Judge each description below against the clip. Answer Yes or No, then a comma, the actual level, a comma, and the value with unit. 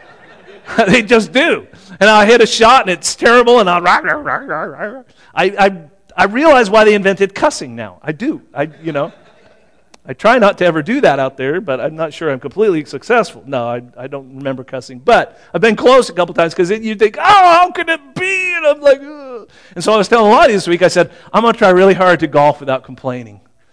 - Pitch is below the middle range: No, high, 195 Hz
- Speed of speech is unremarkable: No, fast, 225 wpm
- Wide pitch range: Yes, wide, 7.9 semitones